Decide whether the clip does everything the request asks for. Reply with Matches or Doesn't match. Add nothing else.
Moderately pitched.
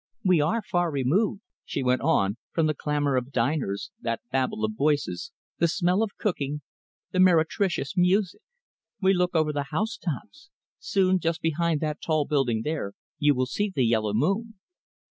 Matches